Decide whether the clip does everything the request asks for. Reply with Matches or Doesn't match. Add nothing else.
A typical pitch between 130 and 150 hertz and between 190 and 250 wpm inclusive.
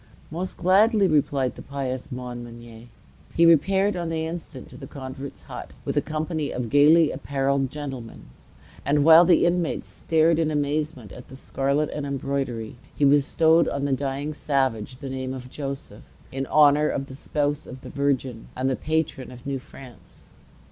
Doesn't match